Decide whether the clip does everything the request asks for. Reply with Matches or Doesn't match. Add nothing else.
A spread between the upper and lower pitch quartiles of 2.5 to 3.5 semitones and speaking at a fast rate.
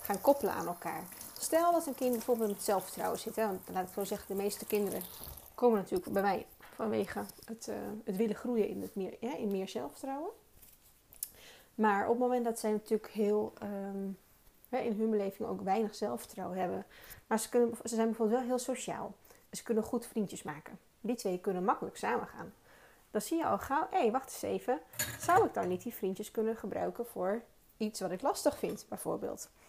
Matches